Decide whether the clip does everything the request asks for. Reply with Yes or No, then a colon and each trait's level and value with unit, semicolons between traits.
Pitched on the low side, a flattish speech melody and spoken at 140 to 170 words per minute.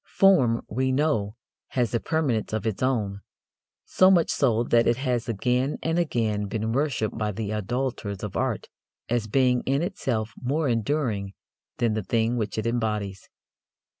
No: low, 115 Hz; average, 3.6 semitones; average, 160 wpm